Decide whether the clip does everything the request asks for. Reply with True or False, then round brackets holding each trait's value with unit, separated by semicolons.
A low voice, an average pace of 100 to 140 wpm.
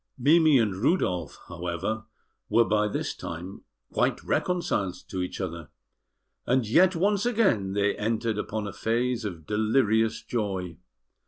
True (110 Hz; 135 wpm)